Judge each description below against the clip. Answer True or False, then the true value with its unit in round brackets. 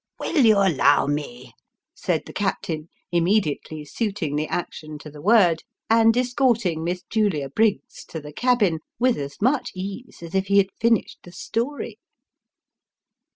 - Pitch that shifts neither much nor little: False (6.2 semitones)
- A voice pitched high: True (195 Hz)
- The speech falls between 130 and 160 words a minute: True (155 wpm)